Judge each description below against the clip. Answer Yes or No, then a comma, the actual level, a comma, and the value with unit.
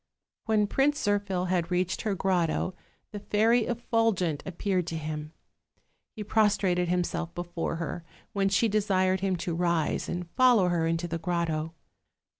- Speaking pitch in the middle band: Yes, medium, 180 Hz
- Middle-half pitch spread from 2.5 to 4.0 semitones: Yes, average, 3.4 semitones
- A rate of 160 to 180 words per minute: No, average, 150 wpm